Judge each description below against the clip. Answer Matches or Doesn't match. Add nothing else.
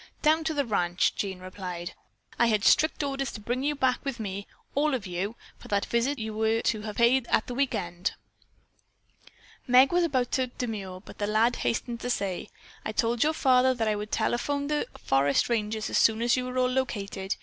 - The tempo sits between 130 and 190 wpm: Doesn't match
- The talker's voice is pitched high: Matches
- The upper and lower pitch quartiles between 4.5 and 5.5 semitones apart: Doesn't match